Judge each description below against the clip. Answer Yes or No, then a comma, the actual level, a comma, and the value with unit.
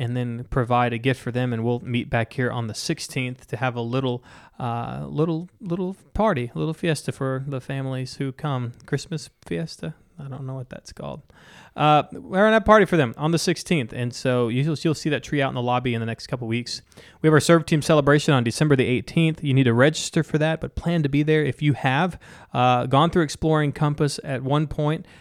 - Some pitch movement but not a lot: Yes, average, 4.1 semitones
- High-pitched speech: No, low, 135 Hz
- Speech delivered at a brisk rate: Yes, fast, 230 wpm